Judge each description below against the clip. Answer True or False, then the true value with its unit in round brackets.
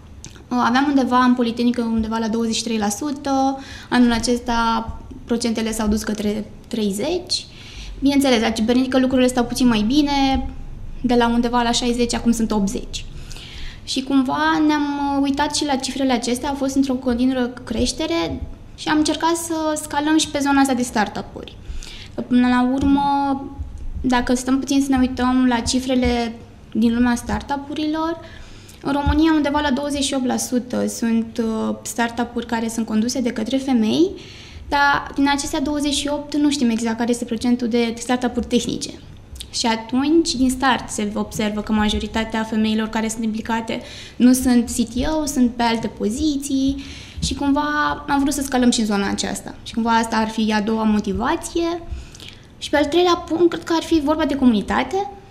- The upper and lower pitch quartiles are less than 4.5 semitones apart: True (3.6 semitones)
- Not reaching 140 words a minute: False (155 wpm)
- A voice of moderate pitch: False (250 Hz)